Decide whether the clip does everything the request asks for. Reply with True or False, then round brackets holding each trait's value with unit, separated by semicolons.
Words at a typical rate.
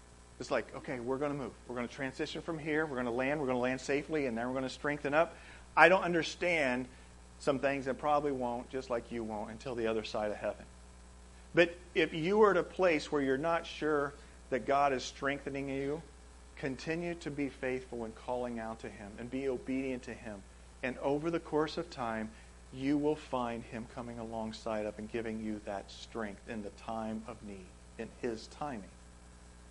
False (210 wpm)